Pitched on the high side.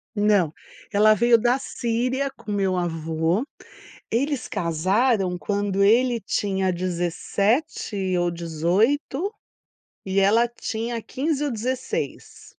Yes: high, 210 Hz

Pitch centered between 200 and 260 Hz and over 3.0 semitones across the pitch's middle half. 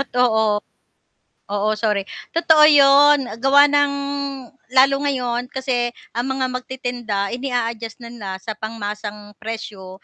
Yes: high, 240 Hz; average, 3.9 semitones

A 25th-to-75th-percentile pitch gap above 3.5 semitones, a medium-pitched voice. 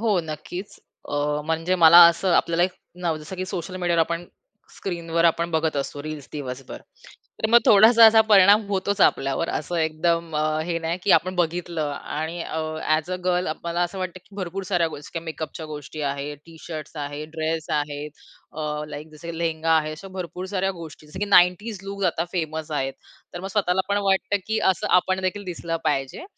No: average, 3.1 semitones; medium, 170 Hz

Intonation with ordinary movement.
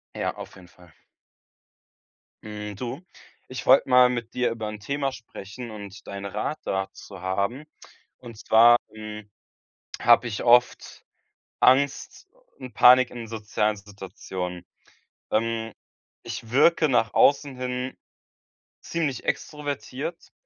Yes: average, 3.5 semitones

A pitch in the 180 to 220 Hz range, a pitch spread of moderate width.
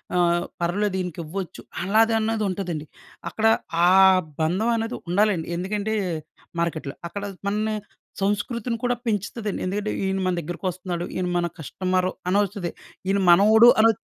Yes: high, 195 Hz; average, 3.5 semitones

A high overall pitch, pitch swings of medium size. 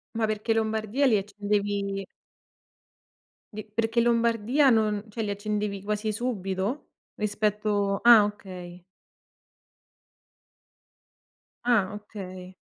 No: high, 210 Hz; narrow, 2.0 semitones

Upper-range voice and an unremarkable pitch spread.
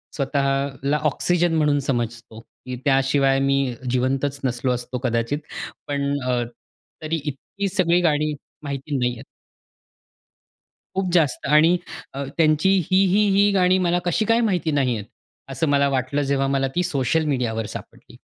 No: medium, 140 Hz; average, 3.7 semitones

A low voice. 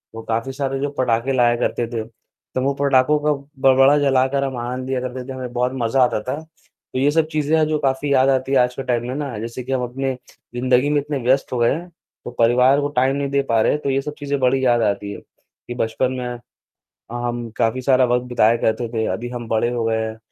Yes: low, 130 Hz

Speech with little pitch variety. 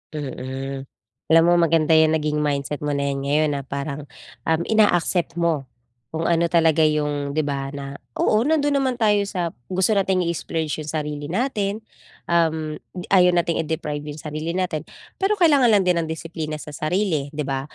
No: average, 3.3 semitones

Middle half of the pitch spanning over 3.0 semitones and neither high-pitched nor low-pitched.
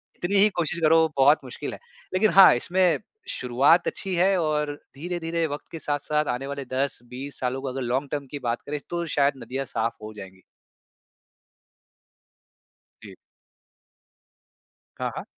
Yes: average, 4.1 semitones; medium, 145 Hz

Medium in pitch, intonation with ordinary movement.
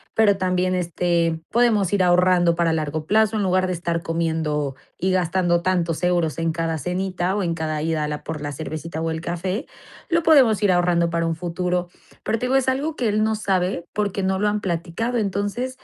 Yes: medium, 180 Hz; average, 3.4 semitones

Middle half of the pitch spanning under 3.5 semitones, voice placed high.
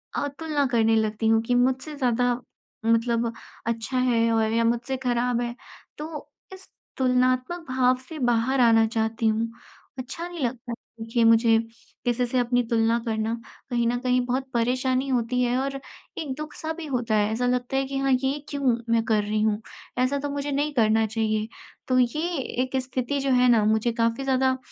Yes: narrow, 2.6 semitones; high, 245 Hz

